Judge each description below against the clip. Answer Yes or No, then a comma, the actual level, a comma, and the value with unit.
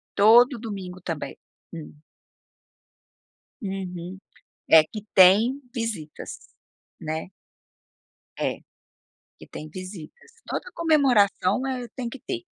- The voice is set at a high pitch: Yes, high, 200 Hz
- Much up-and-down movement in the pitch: Yes, wide, 5.7 semitones